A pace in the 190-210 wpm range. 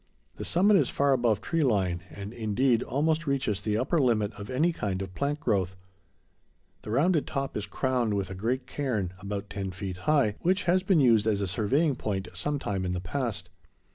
Yes: average, 200 wpm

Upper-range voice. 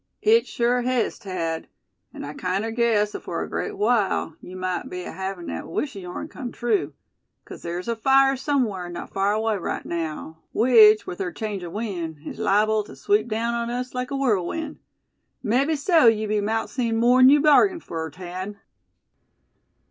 Yes: high, 215 Hz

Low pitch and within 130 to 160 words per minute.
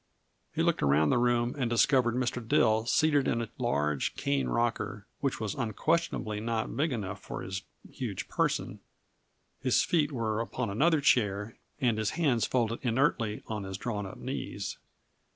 Yes: low, 115 Hz; average, 155 wpm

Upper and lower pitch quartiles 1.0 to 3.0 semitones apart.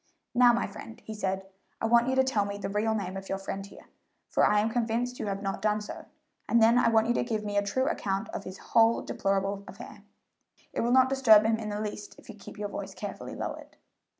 Yes: narrow, 2.6 semitones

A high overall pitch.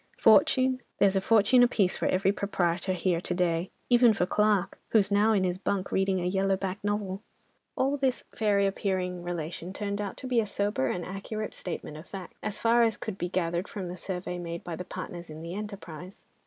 Yes: high, 195 Hz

